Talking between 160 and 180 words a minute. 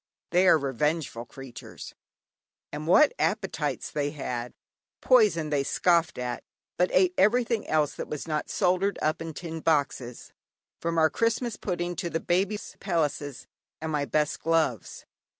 No: average, 145 wpm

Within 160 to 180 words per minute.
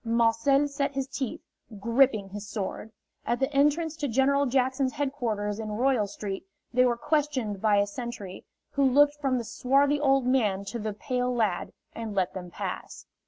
Yes: average, 170 wpm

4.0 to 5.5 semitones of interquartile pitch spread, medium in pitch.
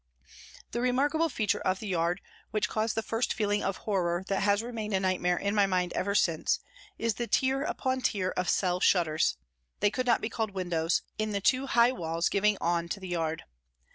No: average, 4.3 semitones; high, 200 Hz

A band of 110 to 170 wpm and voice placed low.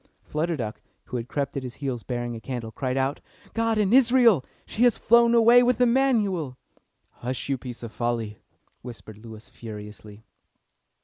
Yes: average, 165 wpm; low, 130 Hz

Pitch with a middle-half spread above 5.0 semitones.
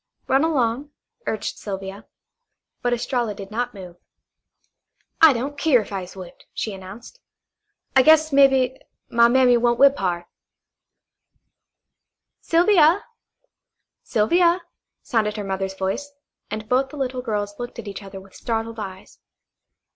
Yes: wide, 5.4 semitones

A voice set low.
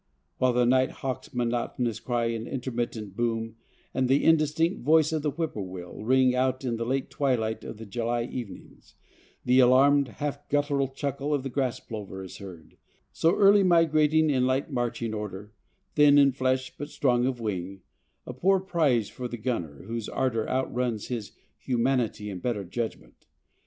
Yes: low, 125 Hz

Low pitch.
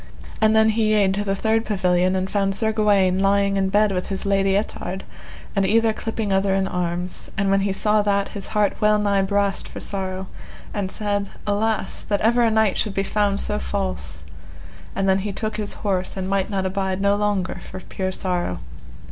No: high, 195 Hz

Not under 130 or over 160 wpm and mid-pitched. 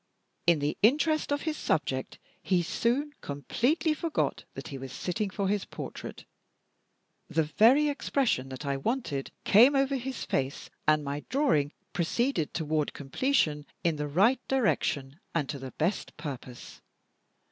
Yes: average, 145 wpm; medium, 175 Hz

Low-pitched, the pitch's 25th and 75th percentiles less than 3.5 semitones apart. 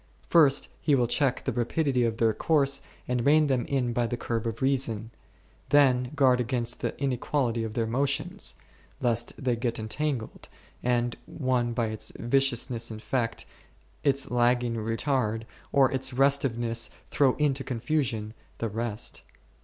Yes: low, 125 Hz; average, 2.9 semitones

